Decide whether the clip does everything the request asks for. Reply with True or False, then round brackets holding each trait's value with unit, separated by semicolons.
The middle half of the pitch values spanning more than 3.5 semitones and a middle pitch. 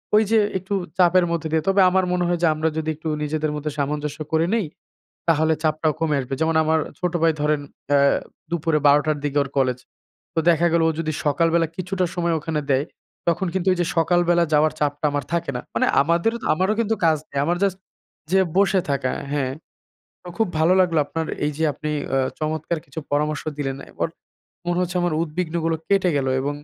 False (2.8 semitones; 160 Hz)